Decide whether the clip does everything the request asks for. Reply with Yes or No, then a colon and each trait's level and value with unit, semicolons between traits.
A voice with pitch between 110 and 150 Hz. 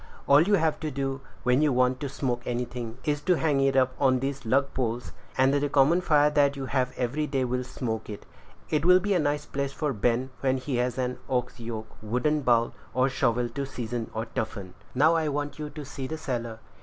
Yes: low, 135 Hz